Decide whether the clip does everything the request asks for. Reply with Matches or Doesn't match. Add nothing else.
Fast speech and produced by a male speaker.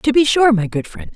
Doesn't match